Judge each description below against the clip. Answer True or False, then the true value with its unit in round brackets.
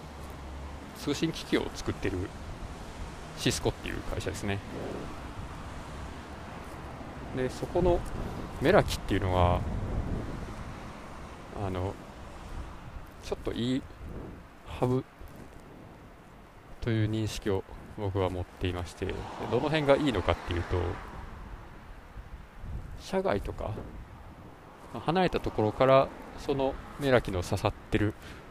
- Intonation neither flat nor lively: True (4.7 semitones)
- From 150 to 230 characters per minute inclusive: True (200 characters per minute)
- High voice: False (95 Hz)